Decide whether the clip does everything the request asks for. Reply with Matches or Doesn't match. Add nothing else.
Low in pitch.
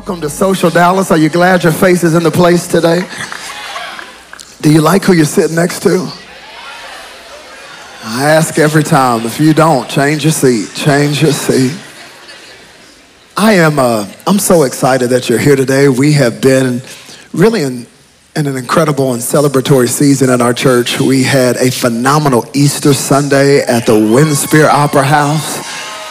Doesn't match